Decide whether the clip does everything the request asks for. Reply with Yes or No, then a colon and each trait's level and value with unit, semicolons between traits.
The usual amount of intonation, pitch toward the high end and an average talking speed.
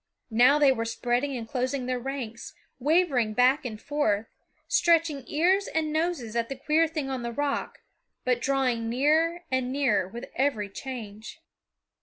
Yes: average, 4.0 semitones; very high, 260 Hz; average, 155 wpm